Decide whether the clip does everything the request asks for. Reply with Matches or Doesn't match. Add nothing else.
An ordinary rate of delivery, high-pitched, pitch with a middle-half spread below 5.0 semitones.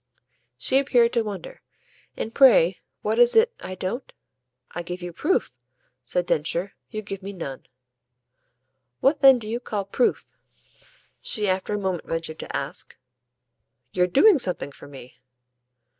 Doesn't match